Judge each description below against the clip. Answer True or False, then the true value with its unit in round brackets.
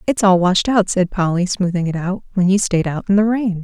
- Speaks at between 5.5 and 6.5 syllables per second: False (5.3 syllables/s)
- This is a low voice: False (190 Hz)